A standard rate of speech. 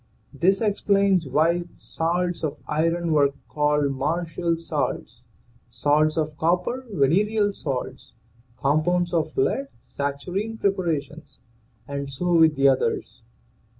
No: slow, 110 wpm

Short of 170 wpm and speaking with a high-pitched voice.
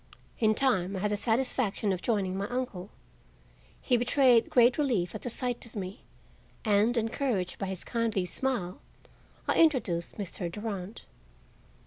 Yes: average, 145 wpm; high, 215 Hz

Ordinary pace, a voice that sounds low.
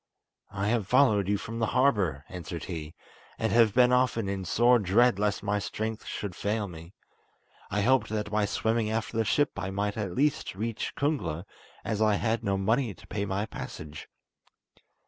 Yes: average, 180 wpm; low, 105 Hz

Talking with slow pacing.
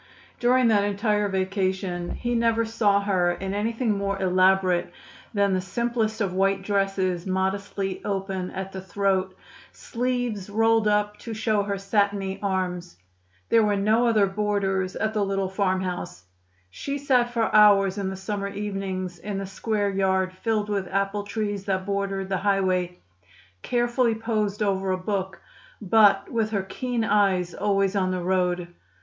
No: average, 155 wpm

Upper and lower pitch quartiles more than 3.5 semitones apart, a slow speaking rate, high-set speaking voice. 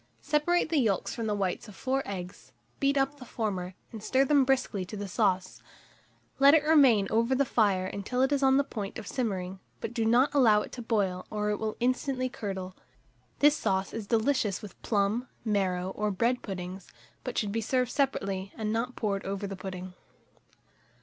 No: average, 4.8 semitones; average, 190 wpm; high, 220 Hz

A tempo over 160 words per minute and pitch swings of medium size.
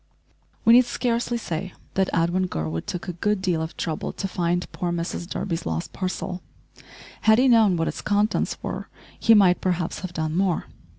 Yes: average, 180 wpm; average, 3.5 semitones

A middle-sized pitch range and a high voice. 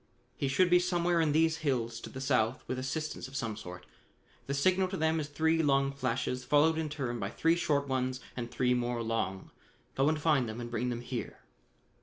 No: average, 4.7 semitones; low, 135 Hz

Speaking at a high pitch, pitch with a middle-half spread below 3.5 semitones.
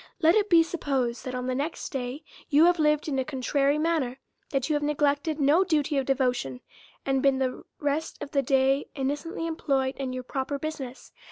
Yes: very high, 280 Hz; average, 2.7 semitones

